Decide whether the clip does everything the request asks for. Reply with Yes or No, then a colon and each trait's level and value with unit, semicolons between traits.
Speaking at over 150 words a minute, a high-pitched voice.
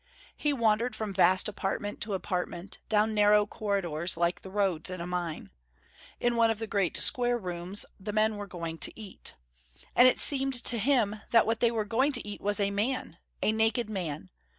Yes: average, 190 wpm; high, 210 Hz